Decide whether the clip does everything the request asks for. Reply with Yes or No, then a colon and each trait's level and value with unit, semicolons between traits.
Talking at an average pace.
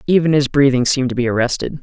No: fast, 230 wpm